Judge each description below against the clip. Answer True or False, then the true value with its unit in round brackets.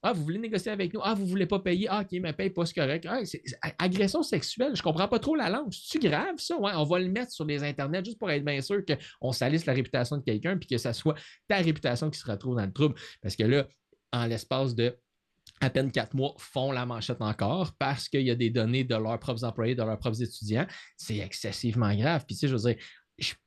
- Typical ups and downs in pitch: False (7.3 semitones)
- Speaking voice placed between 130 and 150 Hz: True (140 Hz)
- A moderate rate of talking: False (260 wpm)